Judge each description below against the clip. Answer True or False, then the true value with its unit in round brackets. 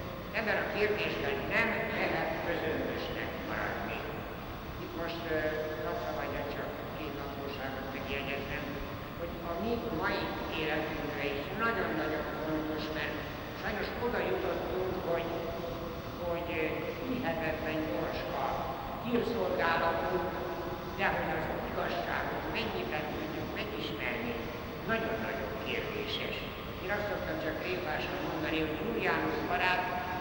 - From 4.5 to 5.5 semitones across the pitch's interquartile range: False (2.7 semitones)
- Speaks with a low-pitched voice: False (165 Hz)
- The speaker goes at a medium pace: False (100 wpm)